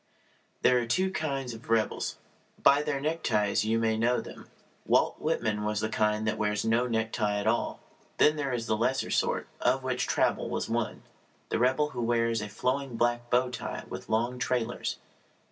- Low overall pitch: Yes, low, 120 Hz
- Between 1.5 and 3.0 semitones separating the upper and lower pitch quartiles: Yes, narrow, 2.6 semitones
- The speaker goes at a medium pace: Yes, average, 185 wpm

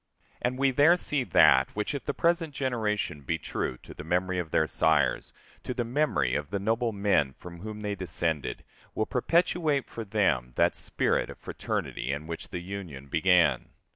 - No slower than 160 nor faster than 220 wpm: Yes, average, 180 wpm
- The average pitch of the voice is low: Yes, low, 100 Hz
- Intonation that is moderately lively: No, wide, 7.8 semitones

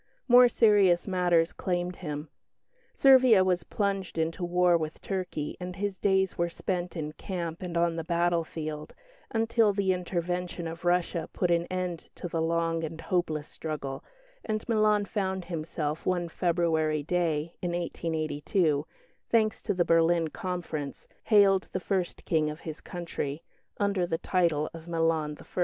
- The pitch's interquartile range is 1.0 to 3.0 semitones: Yes, narrow, 2.4 semitones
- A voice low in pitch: No, medium, 175 Hz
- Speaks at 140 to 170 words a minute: Yes, average, 150 wpm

